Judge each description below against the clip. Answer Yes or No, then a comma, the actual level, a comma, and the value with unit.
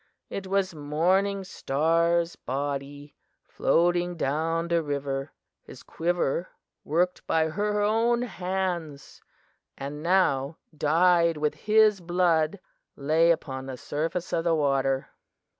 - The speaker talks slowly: Yes, slow, 110 wpm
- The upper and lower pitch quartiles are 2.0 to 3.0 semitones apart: No, average, 3.8 semitones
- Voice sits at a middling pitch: Yes, medium, 165 Hz